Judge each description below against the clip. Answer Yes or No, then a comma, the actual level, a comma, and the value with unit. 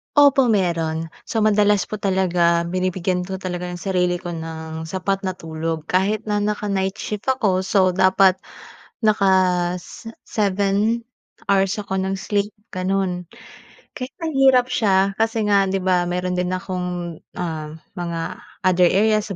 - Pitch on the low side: No, high, 190 Hz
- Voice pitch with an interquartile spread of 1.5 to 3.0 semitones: Yes, narrow, 2.5 semitones